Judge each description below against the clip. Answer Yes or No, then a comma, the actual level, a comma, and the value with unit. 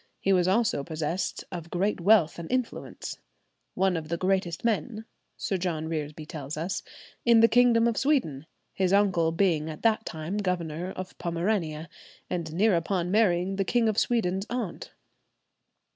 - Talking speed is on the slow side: No, average, 160 wpm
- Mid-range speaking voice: Yes, medium, 180 Hz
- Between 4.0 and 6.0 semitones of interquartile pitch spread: Yes, average, 4.4 semitones